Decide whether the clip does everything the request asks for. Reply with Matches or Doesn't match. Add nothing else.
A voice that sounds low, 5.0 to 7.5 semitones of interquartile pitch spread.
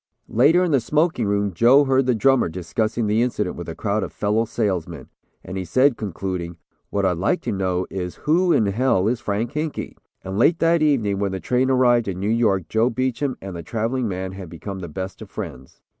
Matches